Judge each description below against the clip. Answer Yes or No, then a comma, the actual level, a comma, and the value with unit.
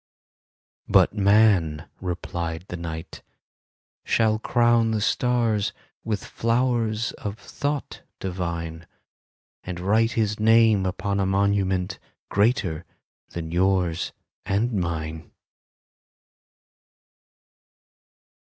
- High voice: No, low, 100 Hz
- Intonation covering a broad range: No, average, 4.3 semitones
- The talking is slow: Yes, slow, 85 wpm